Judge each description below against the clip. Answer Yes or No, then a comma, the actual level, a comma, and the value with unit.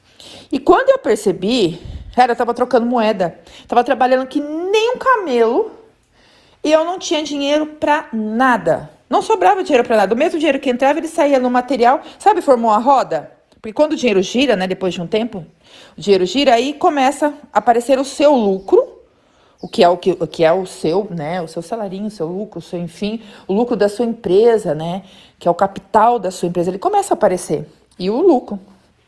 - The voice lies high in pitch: Yes, high, 240 Hz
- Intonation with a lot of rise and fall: Yes, wide, 7.2 semitones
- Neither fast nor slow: No, fast, 205 wpm